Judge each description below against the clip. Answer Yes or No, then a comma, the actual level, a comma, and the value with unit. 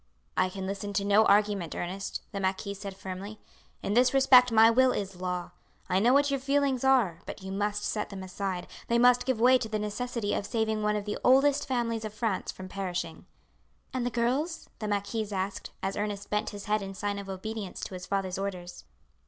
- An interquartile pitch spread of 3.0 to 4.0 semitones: Yes, average, 3.5 semitones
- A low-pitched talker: No, high, 210 Hz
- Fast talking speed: Yes, fast, 210 wpm